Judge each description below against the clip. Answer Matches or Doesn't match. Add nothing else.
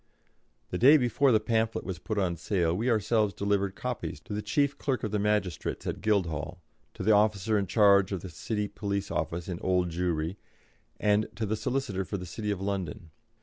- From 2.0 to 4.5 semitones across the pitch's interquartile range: Matches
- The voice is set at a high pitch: Doesn't match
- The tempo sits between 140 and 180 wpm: Doesn't match